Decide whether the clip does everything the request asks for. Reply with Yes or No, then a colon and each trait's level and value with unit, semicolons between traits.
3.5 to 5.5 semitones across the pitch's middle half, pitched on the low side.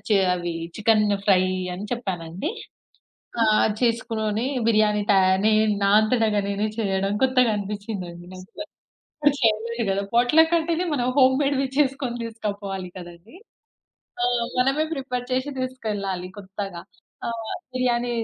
No: average, 4.1 semitones; high, 220 Hz